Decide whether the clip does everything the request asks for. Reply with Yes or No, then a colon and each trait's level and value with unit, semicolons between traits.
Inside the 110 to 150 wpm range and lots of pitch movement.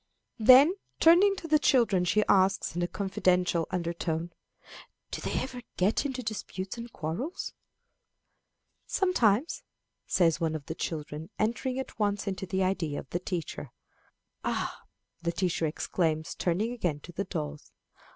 Yes: average, 140 wpm; wide, 6.1 semitones